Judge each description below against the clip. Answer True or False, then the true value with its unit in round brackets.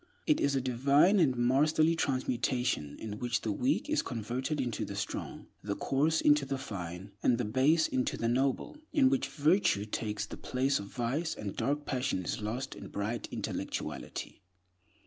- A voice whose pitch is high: False (130 Hz)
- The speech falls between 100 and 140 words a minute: False (170 wpm)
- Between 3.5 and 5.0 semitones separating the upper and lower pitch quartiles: True (4.4 semitones)